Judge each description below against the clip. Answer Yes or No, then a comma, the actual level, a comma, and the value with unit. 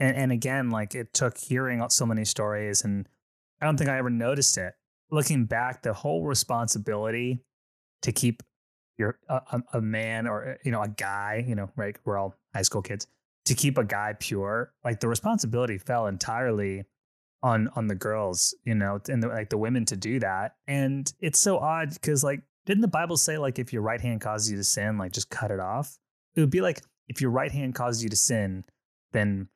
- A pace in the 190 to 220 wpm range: Yes, fast, 205 wpm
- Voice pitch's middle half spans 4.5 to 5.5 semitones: No, average, 3.9 semitones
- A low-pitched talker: Yes, low, 120 Hz